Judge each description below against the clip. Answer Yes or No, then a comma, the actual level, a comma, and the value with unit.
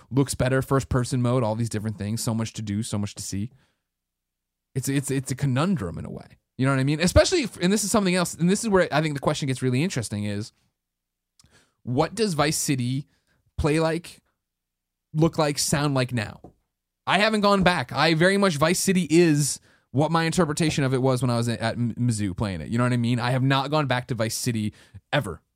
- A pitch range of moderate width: No, wide, 6.4 semitones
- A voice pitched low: Yes, low, 130 Hz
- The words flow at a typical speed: No, fast, 230 wpm